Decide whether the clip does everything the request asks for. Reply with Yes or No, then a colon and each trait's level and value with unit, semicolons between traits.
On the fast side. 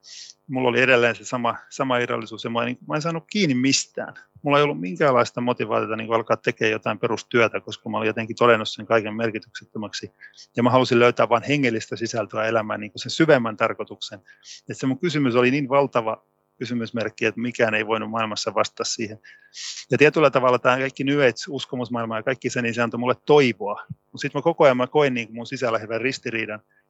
Yes: fast, 195 wpm